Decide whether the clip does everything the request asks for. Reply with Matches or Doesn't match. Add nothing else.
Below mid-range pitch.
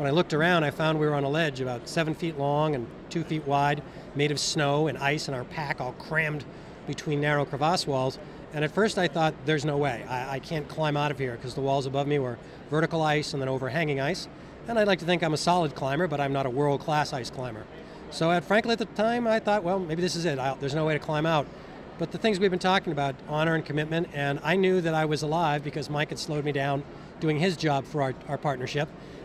Doesn't match